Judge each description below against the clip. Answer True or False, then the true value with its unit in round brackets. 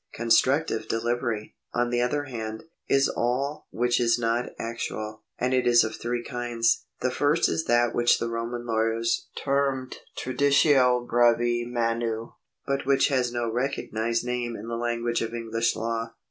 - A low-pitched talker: True (120 Hz)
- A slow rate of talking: False (155 wpm)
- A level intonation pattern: True (1.5 semitones)